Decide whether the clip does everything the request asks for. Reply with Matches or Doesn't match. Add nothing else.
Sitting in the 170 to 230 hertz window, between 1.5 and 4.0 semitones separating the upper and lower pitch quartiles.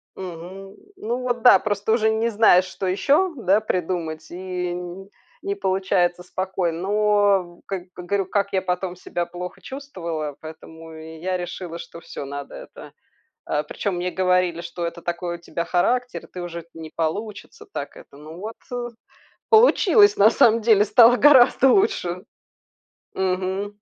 Matches